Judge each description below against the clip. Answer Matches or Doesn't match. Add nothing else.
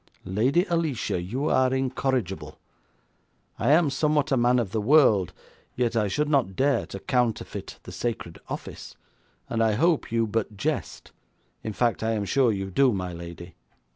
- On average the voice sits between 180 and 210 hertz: Doesn't match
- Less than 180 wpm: Matches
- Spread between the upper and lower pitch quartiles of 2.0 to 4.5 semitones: Doesn't match